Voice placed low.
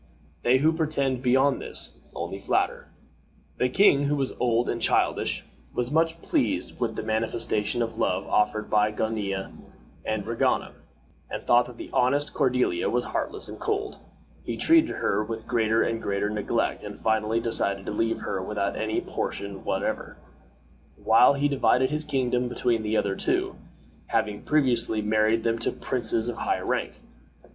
Yes: low, 115 Hz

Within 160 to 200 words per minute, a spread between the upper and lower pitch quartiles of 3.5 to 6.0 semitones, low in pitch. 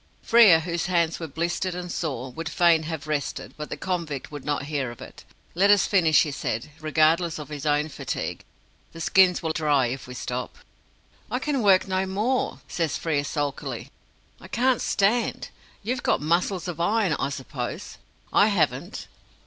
No: average, 175 wpm; average, 4.1 semitones; medium, 165 Hz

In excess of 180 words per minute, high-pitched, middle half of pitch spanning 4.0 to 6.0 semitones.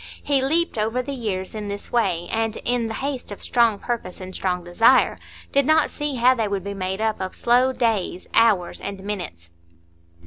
Yes: average, 195 wpm; high, 220 Hz; average, 4.7 semitones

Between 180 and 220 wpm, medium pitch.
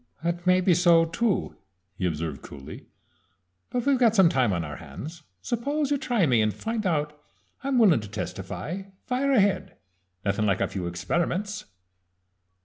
No: average, 160 wpm; medium, 170 Hz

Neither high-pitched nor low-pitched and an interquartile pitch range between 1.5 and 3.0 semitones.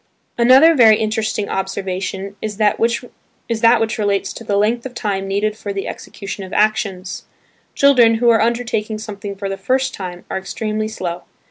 No: high, 215 Hz; average, 2.7 semitones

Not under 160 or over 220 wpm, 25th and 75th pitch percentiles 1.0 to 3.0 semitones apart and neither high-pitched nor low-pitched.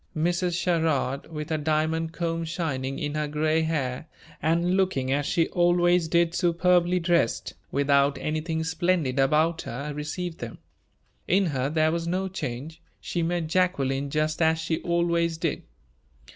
No: average, 145 wpm; narrow, 2.6 semitones; medium, 160 Hz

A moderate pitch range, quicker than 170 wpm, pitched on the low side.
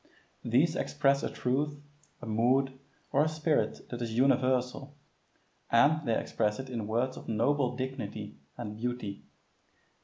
No: average, 3.2 semitones; average, 140 wpm; low, 130 Hz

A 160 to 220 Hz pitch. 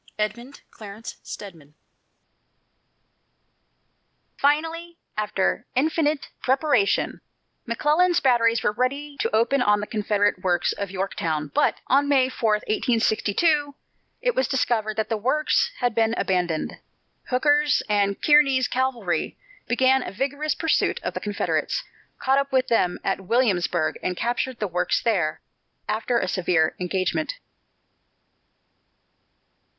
No: high, 235 Hz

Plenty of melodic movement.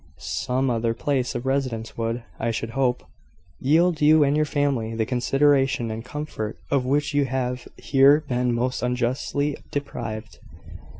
No: average, 3.5 semitones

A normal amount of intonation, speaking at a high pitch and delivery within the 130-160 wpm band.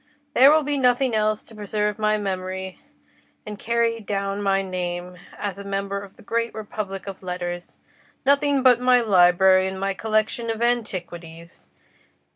Yes: average, 3.5 semitones; high, 205 Hz; average, 150 wpm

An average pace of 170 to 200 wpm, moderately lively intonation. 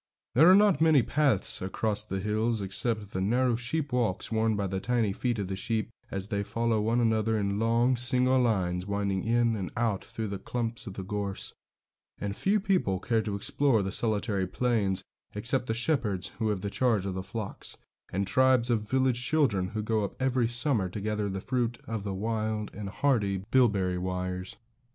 Yes: average, 190 wpm; average, 3.6 semitones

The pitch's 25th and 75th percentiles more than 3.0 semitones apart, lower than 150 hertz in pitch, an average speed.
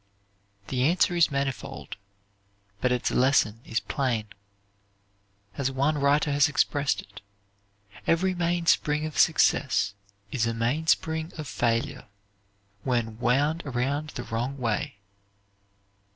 No: average, 4.2 semitones; medium, 140 Hz; slow, 110 wpm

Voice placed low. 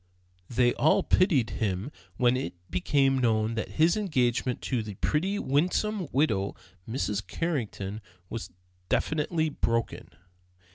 Yes: low, 130 Hz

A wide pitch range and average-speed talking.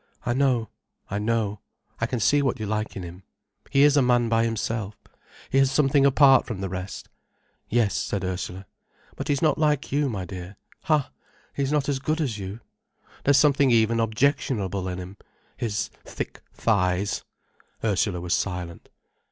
Yes: wide, 5.8 semitones; average, 160 wpm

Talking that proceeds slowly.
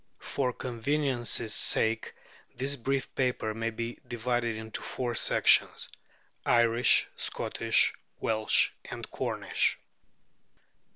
Yes: slow, 95 wpm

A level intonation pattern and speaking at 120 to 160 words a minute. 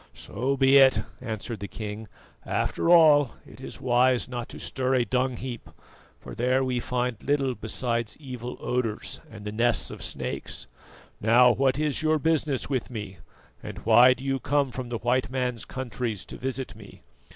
No: narrow, 2.3 semitones; average, 175 wpm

